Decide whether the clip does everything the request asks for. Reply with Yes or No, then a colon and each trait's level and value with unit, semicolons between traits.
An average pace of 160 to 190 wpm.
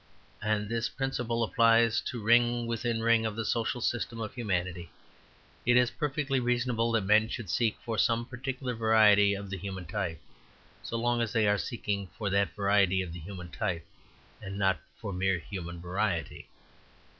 Yes: average, 170 wpm